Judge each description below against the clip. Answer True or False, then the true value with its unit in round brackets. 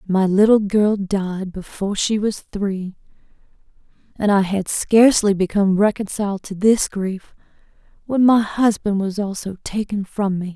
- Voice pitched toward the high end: True (200 Hz)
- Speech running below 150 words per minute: True (140 wpm)